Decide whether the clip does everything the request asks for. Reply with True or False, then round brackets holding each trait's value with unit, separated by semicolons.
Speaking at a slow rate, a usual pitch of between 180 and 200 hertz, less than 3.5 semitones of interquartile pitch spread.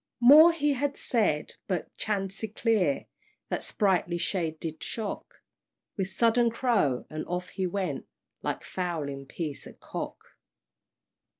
False (120 wpm; 190 Hz; 5.6 semitones)